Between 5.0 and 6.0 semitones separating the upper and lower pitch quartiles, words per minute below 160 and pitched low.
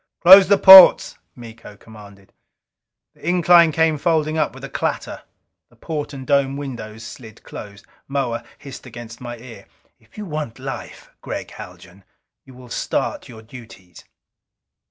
Yes: wide, 5.5 semitones; average, 145 wpm; low, 130 Hz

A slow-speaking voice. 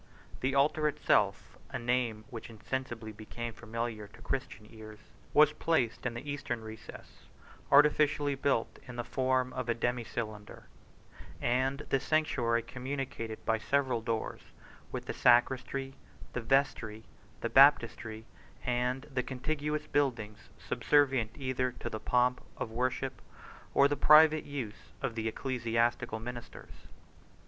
Yes: slow, 130 wpm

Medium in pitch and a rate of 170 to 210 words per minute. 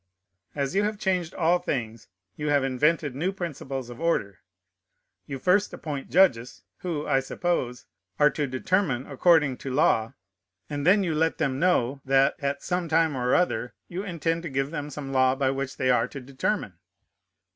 Yes: medium, 145 Hz; average, 175 wpm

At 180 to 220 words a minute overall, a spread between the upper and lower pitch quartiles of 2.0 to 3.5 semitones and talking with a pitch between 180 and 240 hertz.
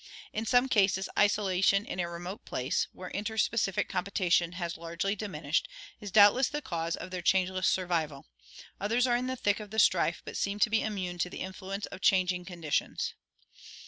Yes: average, 185 wpm; average, 2.8 semitones; high, 190 Hz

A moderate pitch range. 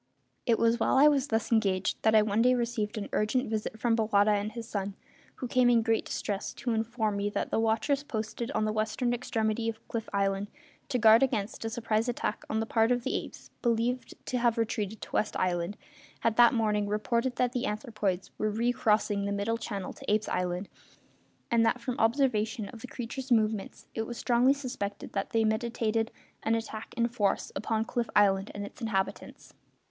No: narrow, 2.2 semitones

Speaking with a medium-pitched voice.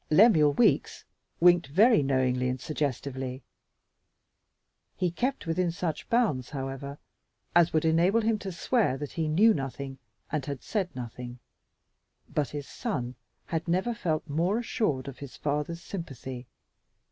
Yes: medium, 155 Hz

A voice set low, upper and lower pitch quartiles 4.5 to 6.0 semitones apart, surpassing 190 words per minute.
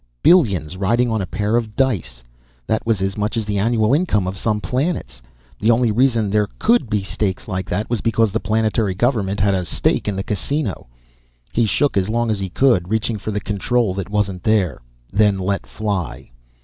No: low, 105 Hz; average, 3.0 semitones; average, 200 wpm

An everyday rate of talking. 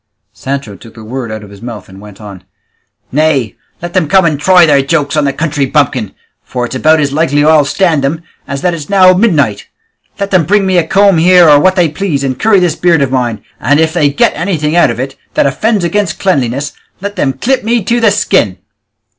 No: fast, 225 wpm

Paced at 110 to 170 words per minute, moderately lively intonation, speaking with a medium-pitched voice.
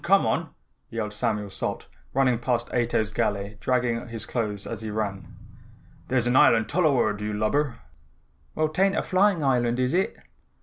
No: average, 165 wpm; average, 3.6 semitones; low, 120 Hz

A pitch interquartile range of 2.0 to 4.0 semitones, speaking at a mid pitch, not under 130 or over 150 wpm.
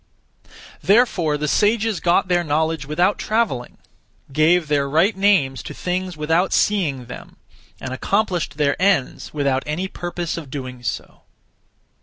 No: average, 4.8 semitones; medium, 165 Hz; slow, 135 wpm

